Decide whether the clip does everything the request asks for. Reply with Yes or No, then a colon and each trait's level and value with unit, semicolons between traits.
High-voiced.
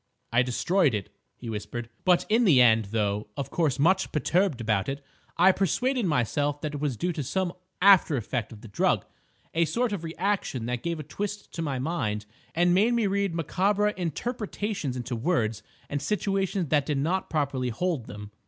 No: medium, 155 Hz